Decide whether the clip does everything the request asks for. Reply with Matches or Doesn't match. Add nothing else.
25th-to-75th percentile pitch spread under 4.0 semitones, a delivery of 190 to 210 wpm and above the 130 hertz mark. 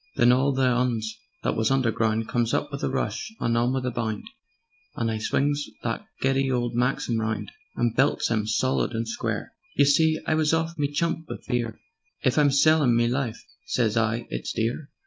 Doesn't match